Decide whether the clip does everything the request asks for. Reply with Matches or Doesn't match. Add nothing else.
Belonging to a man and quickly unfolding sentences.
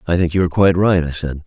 Matches